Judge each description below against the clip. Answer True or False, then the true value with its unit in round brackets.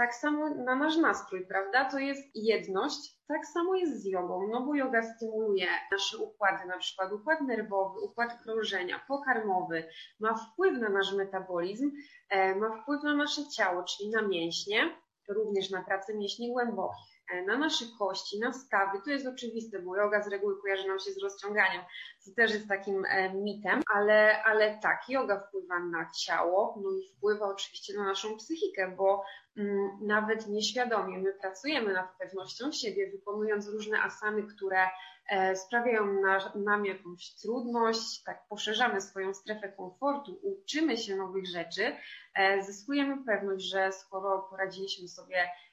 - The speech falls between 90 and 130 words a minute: False (155 wpm)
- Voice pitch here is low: False (205 Hz)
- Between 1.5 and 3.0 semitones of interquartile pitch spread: False (3.9 semitones)